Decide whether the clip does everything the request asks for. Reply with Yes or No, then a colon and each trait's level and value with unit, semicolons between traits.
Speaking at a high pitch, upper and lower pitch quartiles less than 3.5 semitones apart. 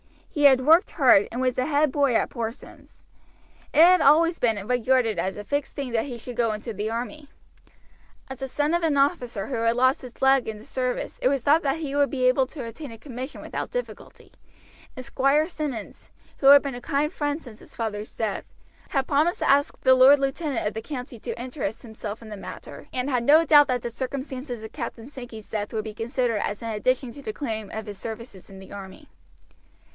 No: very high, 255 Hz; average, 4.0 semitones